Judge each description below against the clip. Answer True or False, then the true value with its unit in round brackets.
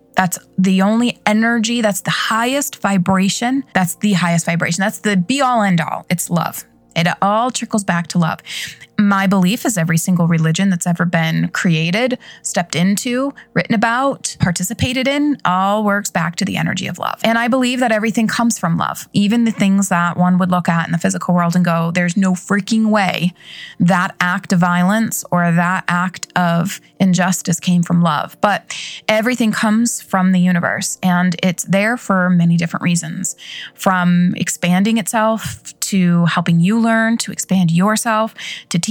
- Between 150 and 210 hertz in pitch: True (190 Hz)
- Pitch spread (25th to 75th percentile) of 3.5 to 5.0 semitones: True (3.8 semitones)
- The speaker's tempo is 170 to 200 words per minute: True (175 wpm)